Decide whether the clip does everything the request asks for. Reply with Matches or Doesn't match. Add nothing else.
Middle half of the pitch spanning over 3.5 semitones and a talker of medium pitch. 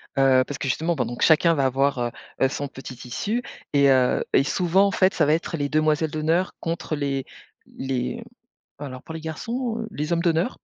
Matches